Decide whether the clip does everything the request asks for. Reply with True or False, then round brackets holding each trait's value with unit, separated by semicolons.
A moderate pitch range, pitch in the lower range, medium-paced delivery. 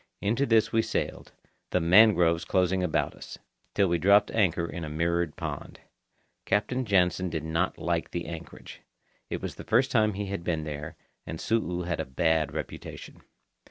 True (3.8 semitones; 90 Hz; 170 wpm)